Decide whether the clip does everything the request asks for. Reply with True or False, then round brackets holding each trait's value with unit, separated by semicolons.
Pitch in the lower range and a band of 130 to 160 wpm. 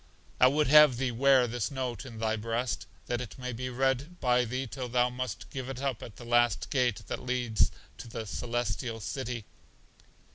False (125 Hz; 190 wpm)